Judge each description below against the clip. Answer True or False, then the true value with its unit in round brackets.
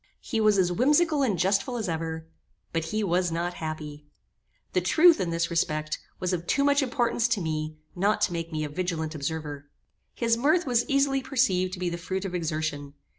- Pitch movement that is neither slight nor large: False (6.5 semitones)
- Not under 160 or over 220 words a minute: True (195 wpm)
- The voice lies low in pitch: False (180 Hz)